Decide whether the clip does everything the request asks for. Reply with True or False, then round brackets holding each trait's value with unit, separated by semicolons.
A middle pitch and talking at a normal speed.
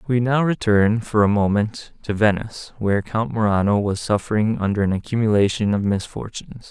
False (105 Hz; 160 wpm)